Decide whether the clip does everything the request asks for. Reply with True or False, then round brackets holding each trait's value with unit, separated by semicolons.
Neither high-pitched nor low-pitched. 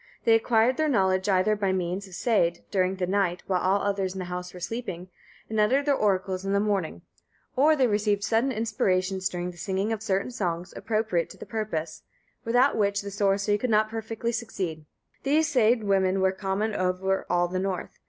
False (200 Hz)